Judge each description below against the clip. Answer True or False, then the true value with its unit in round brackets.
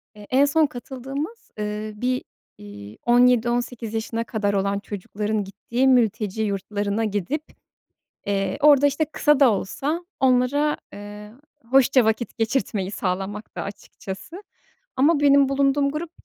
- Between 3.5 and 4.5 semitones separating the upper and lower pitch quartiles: False (5.0 semitones)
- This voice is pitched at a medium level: False (235 Hz)